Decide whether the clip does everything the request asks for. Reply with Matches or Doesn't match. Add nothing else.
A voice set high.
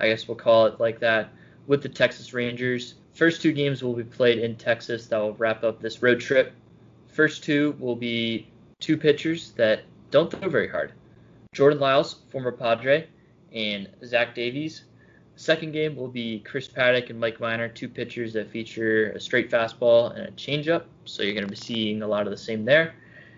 Doesn't match